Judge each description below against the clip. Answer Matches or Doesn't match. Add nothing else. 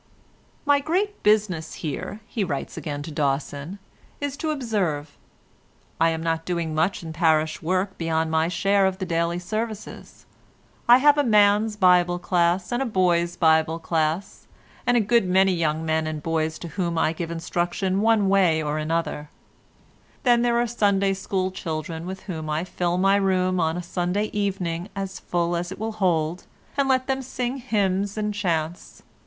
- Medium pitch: Matches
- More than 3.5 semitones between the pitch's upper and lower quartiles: Matches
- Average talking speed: Matches